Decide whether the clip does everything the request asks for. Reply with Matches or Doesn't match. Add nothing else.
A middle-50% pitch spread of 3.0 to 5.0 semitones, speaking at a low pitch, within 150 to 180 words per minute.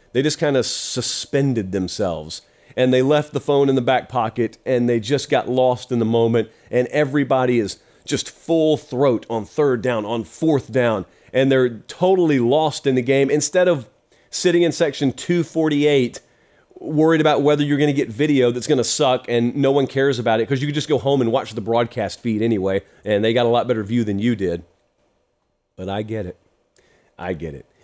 Doesn't match